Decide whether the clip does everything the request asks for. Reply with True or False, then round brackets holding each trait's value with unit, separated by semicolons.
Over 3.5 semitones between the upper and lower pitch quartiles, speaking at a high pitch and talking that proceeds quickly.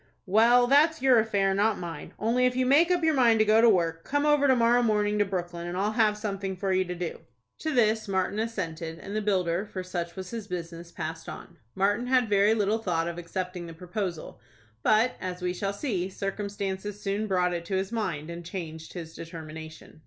True (4.2 semitones; 195 Hz; 210 wpm)